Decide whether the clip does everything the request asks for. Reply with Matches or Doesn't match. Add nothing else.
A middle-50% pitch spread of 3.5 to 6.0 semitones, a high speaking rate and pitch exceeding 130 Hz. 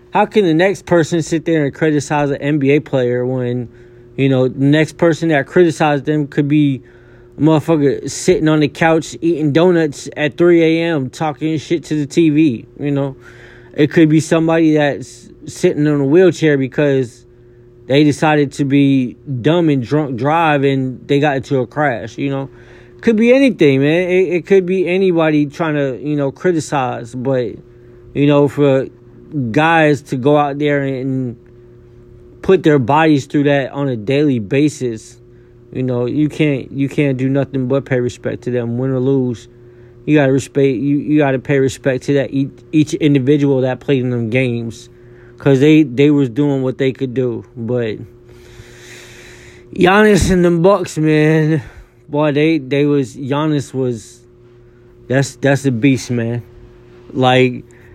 Doesn't match